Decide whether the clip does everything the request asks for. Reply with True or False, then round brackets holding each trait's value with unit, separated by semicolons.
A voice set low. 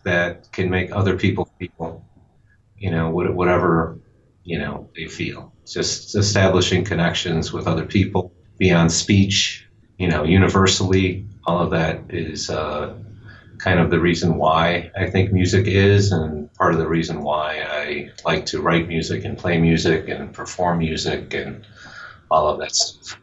True (90 Hz)